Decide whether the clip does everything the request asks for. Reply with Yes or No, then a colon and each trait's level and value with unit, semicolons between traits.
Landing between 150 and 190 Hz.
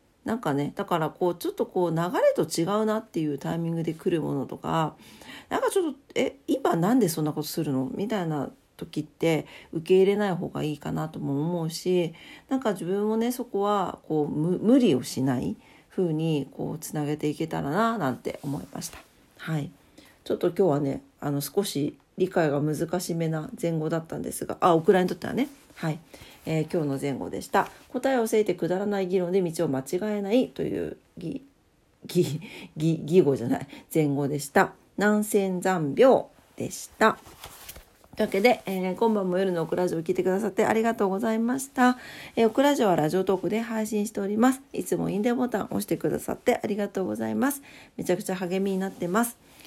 Yes: medium, 185 Hz